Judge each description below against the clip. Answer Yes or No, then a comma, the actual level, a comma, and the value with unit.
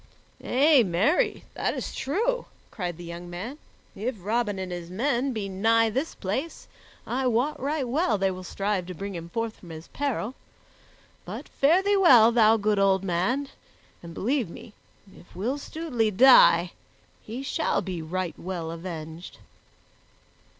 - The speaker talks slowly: No, average, 155 wpm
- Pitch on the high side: Yes, high, 215 Hz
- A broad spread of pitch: Yes, wide, 6.5 semitones